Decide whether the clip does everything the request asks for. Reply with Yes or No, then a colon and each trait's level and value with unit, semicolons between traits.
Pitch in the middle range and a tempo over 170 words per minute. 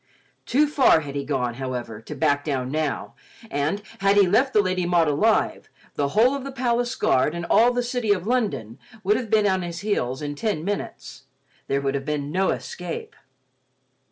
Yes: medium, 175 Hz; average, 190 wpm